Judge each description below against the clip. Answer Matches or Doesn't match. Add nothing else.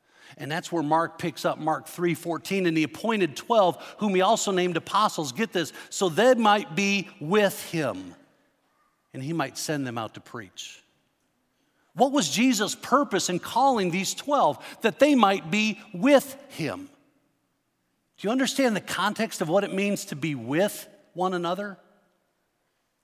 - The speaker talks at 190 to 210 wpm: Doesn't match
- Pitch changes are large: Matches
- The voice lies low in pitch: Doesn't match